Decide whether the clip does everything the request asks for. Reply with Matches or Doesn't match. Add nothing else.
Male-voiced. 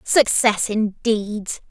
Doesn't match